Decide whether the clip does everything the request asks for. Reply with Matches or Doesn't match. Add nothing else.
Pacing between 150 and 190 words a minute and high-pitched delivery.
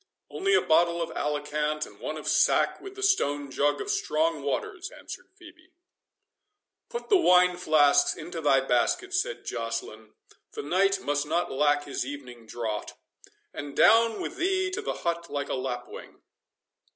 Doesn't match